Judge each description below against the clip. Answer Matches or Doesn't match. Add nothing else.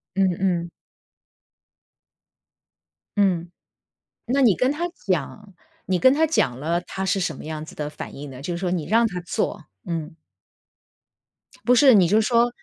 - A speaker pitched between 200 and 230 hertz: Doesn't match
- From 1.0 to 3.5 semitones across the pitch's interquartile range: Doesn't match